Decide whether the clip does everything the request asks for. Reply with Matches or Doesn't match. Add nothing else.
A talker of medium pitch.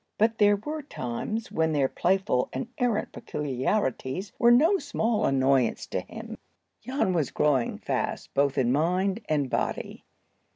Matches